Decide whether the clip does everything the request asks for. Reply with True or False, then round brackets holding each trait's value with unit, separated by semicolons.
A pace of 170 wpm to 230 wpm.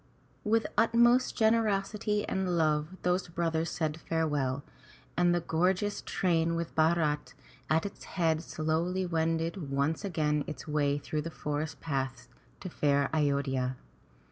False (140 wpm)